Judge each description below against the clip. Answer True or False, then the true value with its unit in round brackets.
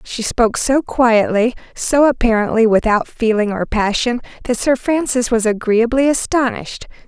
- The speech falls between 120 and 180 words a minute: True (135 wpm)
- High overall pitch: True (235 Hz)